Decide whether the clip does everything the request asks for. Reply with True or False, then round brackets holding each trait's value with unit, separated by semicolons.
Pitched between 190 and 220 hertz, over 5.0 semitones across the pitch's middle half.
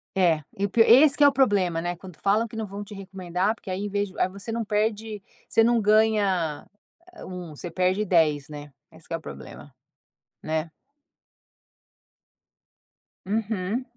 False (195 Hz; 3.7 semitones)